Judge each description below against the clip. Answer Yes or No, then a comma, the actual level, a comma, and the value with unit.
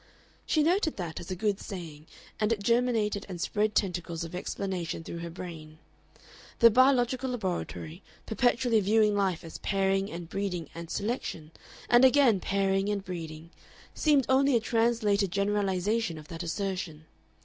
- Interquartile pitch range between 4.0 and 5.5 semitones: Yes, average, 5.0 semitones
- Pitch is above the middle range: Yes, high, 195 Hz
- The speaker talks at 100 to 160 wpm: Yes, average, 150 wpm